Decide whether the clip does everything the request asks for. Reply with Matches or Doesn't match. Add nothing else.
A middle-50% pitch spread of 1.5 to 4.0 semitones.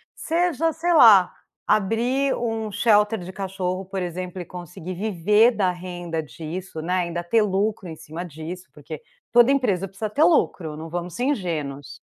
Doesn't match